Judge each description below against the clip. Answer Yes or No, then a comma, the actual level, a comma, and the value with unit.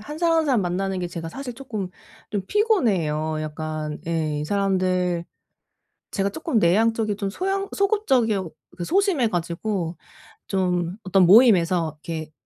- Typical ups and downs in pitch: No, wide, 6.0 semitones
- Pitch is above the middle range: Yes, high, 195 Hz